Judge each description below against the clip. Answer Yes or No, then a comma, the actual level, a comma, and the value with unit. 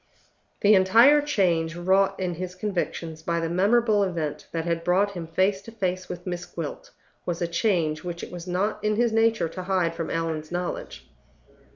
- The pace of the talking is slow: No, average, 185 wpm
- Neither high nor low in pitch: Yes, medium, 180 Hz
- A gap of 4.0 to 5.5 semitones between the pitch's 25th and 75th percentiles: No, average, 3.2 semitones